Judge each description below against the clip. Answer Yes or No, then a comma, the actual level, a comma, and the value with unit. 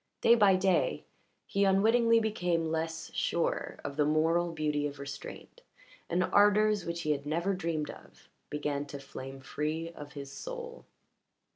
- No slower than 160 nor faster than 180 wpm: No, average, 150 wpm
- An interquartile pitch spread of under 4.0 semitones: No, average, 5.0 semitones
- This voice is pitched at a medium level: Yes, medium, 165 Hz